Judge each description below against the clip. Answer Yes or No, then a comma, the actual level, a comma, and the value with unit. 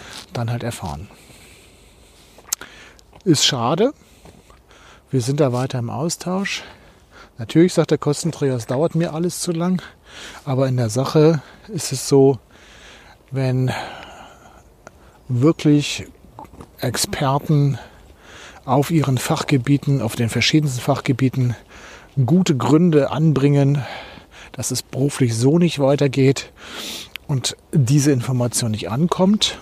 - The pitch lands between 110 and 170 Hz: Yes, medium, 140 Hz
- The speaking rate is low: Yes, slow, 105 wpm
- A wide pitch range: No, average, 3.7 semitones